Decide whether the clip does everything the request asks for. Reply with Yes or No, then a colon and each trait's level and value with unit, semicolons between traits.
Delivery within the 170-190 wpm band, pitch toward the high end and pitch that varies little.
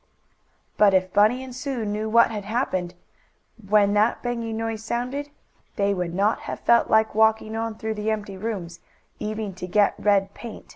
Yes: average, 175 wpm; high, 215 Hz; narrow, 2.0 semitones